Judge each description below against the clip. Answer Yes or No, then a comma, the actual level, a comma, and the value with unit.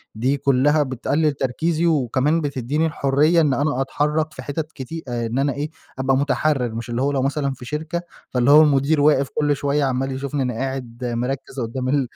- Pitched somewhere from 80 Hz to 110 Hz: No, medium, 140 Hz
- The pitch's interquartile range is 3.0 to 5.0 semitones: No, narrow, 2.6 semitones